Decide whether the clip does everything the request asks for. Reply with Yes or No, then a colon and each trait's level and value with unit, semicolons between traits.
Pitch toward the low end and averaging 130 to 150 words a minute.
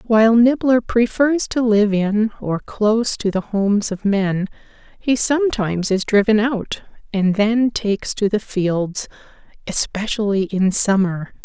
No: high, 210 Hz; average, 140 wpm